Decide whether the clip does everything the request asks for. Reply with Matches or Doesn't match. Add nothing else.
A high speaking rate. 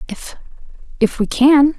Doesn't match